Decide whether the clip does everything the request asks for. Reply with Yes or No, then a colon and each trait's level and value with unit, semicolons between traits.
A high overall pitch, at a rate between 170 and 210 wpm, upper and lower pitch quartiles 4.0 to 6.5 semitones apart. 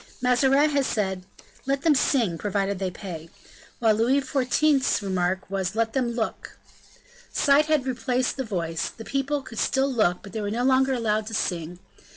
Yes: high, 230 Hz; average, 175 wpm; wide, 5.5 semitones